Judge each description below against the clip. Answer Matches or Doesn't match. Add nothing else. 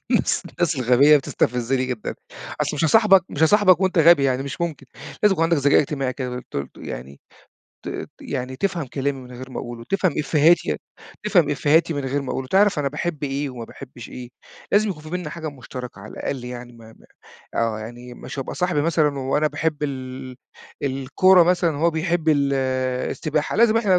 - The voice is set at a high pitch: Doesn't match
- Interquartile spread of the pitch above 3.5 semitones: Matches